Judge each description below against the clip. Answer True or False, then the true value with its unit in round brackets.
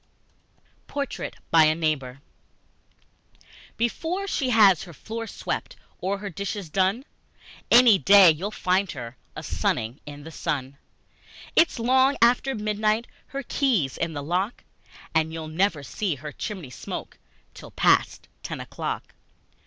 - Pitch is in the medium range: False (195 Hz)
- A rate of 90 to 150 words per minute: True (135 wpm)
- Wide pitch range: True (6.7 semitones)